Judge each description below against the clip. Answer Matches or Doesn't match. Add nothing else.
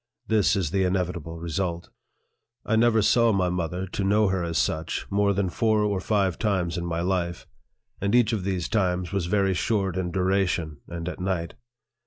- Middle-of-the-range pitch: Doesn't match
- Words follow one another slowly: Doesn't match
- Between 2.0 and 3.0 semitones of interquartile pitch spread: Matches